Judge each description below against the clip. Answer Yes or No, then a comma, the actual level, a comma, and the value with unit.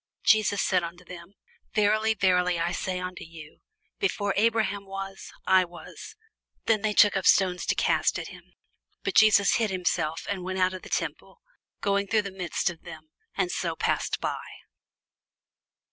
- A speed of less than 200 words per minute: Yes, average, 165 wpm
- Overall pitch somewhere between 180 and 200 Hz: Yes, high, 190 Hz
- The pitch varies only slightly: Yes, narrow, 2.3 semitones